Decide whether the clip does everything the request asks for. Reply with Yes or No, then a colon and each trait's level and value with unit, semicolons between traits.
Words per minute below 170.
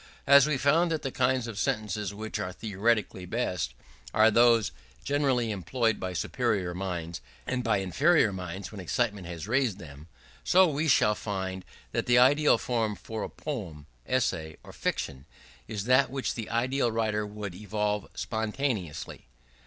Yes: average, 155 wpm